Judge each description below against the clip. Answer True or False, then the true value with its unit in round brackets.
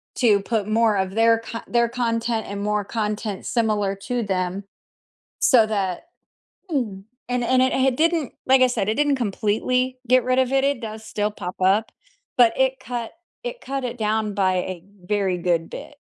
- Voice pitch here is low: False (225 Hz)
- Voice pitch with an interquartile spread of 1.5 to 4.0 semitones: True (3.7 semitones)